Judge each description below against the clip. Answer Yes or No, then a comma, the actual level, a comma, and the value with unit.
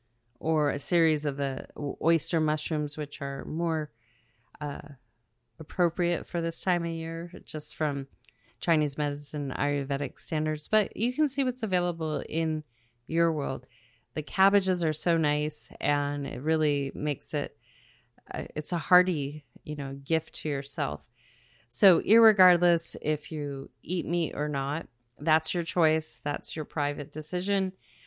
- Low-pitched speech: No, medium, 155 Hz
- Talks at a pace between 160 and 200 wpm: No, average, 140 wpm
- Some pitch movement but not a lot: Yes, average, 3.1 semitones